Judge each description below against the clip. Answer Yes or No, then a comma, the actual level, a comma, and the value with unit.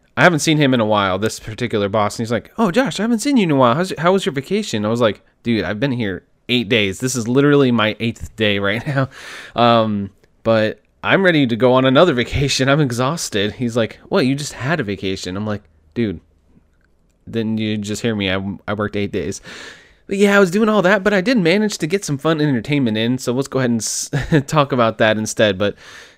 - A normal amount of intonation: No, wide, 5.8 semitones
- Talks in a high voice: No, low, 120 Hz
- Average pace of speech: No, fast, 240 wpm